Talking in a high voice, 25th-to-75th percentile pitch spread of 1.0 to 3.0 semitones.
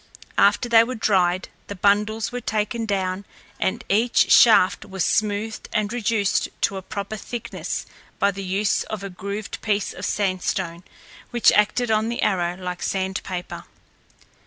Yes: high, 205 Hz; narrow, 2.6 semitones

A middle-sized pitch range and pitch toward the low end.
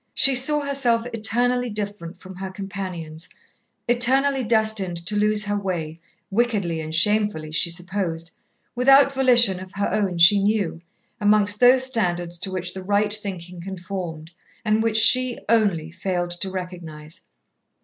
No: average, 4.3 semitones; high, 200 Hz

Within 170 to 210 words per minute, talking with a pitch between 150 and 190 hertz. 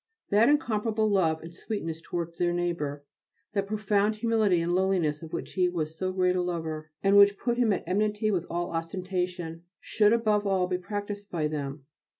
Yes: average, 180 wpm; medium, 185 Hz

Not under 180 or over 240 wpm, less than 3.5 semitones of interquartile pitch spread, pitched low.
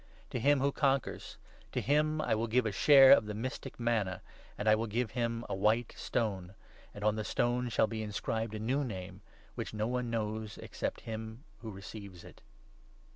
Yes: average, 195 wpm; average, 2.7 semitones; low, 110 Hz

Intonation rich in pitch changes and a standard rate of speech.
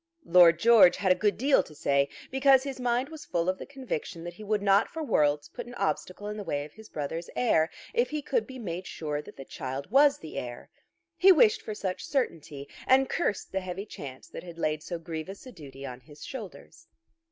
No: wide, 8.2 semitones; fast, 220 wpm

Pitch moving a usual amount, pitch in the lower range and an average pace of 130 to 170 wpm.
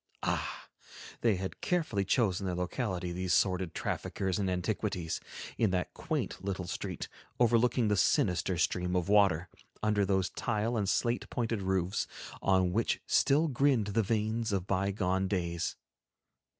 Yes: average, 3.4 semitones; low, 100 Hz; average, 140 wpm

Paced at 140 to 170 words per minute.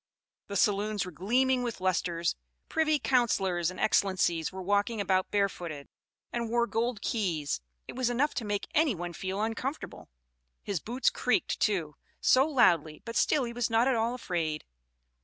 Yes: average, 160 wpm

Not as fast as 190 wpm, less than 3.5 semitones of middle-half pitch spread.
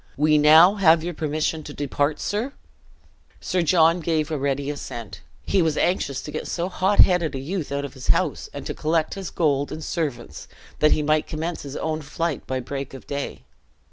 No: average, 200 wpm; average, 2.9 semitones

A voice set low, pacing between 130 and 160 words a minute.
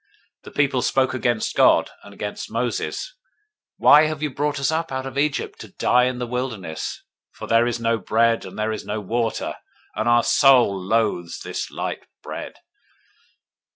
No: low, 120 Hz; average, 175 wpm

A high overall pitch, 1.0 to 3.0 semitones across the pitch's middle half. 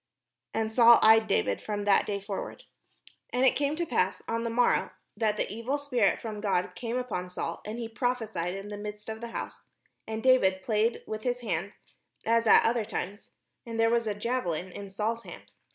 Yes: high, 220 Hz; narrow, 2.6 semitones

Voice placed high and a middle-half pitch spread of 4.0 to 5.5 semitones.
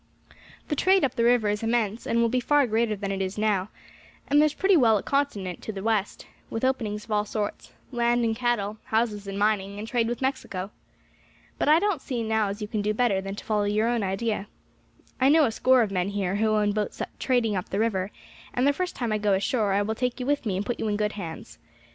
No: high, 220 Hz; average, 3.0 semitones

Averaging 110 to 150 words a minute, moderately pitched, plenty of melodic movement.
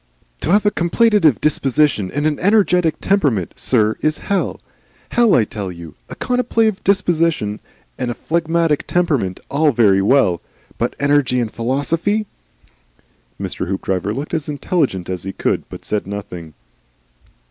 Yes: average, 145 wpm; medium, 145 Hz; wide, 8.8 semitones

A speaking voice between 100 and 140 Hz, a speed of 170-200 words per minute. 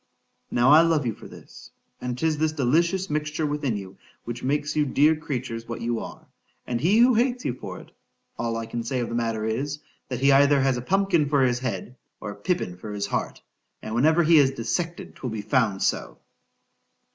Yes: low, 135 Hz; average, 190 wpm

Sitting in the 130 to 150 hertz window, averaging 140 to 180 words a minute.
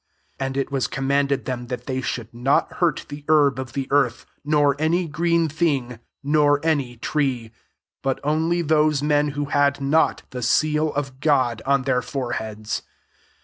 Yes: medium, 140 Hz; average, 170 wpm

